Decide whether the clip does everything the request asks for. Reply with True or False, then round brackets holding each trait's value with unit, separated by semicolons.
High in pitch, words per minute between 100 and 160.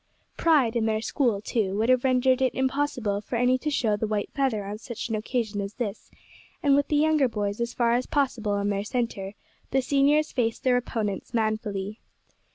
False (235 Hz; 195 wpm)